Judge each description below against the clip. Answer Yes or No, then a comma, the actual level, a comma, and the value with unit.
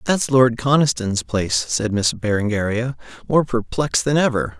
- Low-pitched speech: Yes, low, 120 Hz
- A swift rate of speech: No, average, 145 wpm